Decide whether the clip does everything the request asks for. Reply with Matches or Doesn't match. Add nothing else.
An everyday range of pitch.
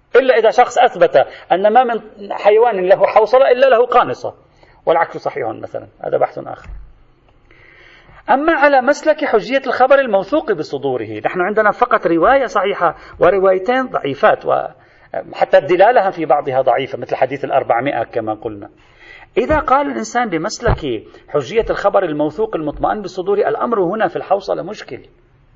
Doesn't match